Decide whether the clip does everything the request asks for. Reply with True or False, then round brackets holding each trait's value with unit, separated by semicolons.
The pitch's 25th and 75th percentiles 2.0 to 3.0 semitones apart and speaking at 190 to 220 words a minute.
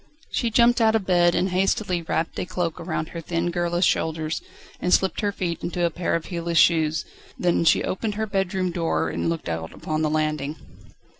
True (2.5 semitones; 200 wpm)